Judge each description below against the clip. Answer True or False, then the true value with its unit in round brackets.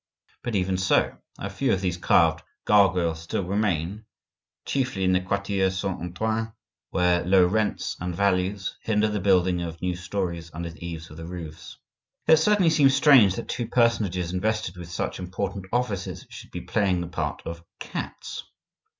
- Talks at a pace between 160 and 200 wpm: True (165 wpm)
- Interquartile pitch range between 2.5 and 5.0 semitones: True (3.2 semitones)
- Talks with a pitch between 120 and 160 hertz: False (95 Hz)